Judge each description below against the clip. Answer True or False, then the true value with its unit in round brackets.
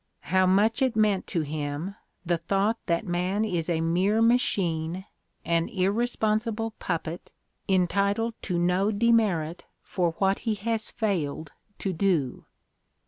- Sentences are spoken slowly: True (130 wpm)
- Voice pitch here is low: False (190 Hz)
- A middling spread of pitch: True (4.2 semitones)